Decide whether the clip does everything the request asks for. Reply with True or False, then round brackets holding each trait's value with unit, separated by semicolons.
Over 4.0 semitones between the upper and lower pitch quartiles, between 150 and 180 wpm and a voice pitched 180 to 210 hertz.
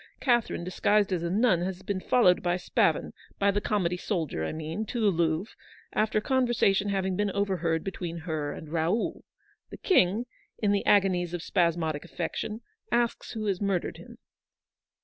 False (3.5 semitones; 175 wpm; 190 Hz)